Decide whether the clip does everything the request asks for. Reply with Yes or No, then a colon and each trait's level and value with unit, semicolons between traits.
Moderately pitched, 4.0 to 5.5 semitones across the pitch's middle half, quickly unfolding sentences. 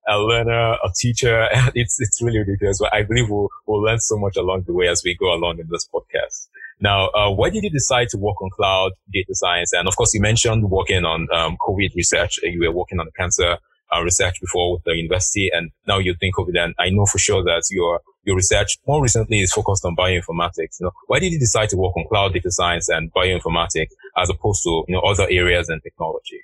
No: low, 100 Hz; average, 4.3 semitones; fast, 230 wpm